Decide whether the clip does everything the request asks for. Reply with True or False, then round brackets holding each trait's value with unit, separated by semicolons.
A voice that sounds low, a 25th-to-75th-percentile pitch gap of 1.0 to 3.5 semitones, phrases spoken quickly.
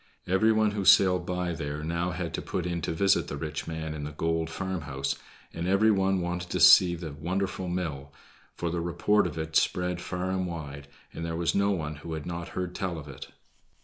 True (85 Hz; 2.6 semitones; 215 wpm)